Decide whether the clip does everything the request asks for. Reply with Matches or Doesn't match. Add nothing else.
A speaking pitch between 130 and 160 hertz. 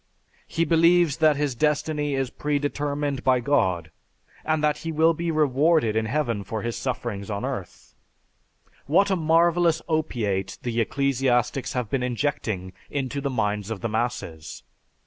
Matches